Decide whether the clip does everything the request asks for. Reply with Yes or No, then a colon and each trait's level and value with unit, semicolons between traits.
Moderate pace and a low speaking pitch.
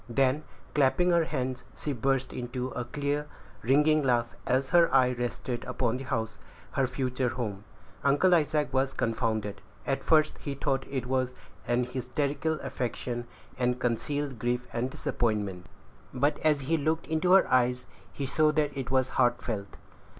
Yes: average, 155 wpm; low, 130 Hz